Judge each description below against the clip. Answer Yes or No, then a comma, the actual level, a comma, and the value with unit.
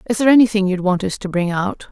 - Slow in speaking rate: No, fast, 280 wpm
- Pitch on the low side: No, high, 200 Hz